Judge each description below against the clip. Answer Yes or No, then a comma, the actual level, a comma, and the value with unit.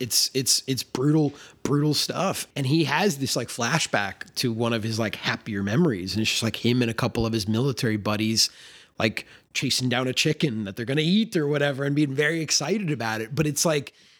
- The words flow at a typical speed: No, fast, 220 wpm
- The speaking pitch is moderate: No, low, 130 Hz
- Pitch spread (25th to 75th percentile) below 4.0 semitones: No, average, 4.7 semitones